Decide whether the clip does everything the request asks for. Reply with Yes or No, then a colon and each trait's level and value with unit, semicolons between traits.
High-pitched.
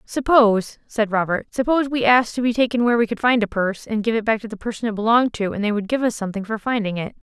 Yes: high, 225 Hz